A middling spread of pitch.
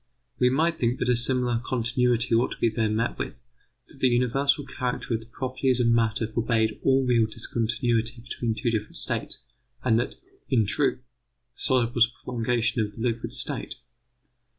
No: narrow, 1.7 semitones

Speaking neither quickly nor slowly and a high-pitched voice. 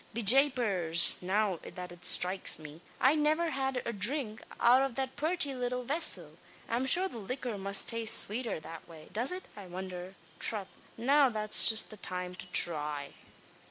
Yes: average, 165 wpm; high, 220 Hz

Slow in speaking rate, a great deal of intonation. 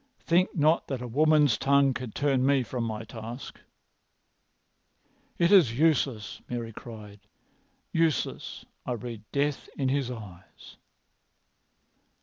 No: slow, 120 wpm; average, 4.3 semitones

